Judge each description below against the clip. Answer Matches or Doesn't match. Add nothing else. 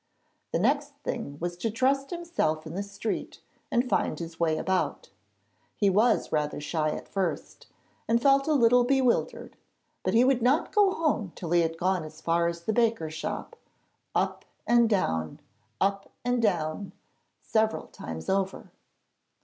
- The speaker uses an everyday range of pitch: Doesn't match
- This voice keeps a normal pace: Matches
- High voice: Matches